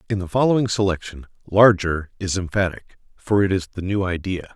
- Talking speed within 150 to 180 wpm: Yes, average, 170 wpm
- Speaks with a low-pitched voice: Yes, very low, 95 Hz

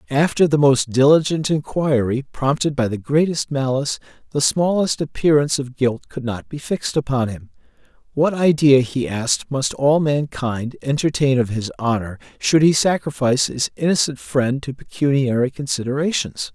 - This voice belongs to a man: Yes, male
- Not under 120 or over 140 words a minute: No, average, 150 wpm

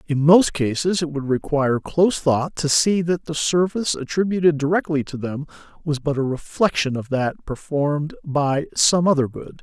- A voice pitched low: No, medium, 150 Hz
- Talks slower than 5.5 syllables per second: Yes, 5.0 syllables/s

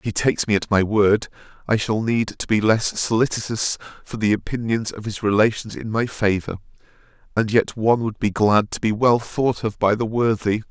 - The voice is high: No, low, 110 Hz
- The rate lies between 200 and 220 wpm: Yes, fast, 205 wpm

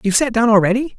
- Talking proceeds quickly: Yes, fast, 245 wpm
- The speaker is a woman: No, male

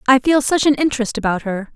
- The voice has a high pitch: Yes, very high, 250 Hz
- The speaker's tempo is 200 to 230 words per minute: No, fast, 240 wpm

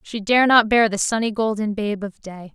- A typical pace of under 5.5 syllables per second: Yes, 4.9 syllables/s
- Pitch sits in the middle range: No, high, 215 Hz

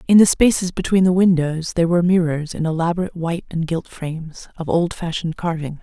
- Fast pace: No, average, 185 wpm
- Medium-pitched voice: Yes, medium, 170 Hz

